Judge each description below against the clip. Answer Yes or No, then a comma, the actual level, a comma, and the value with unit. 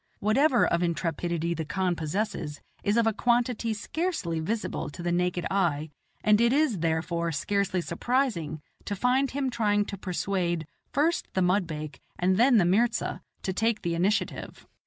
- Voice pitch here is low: No, high, 190 Hz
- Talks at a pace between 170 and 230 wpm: No, average, 155 wpm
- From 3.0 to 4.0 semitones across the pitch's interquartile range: No, average, 5.3 semitones